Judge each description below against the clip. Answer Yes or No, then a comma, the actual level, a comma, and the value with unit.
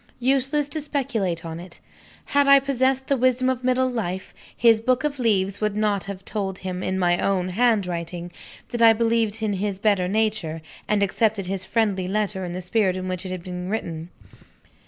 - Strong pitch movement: No, average, 4.5 semitones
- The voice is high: Yes, high, 205 Hz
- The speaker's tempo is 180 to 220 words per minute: Yes, average, 185 wpm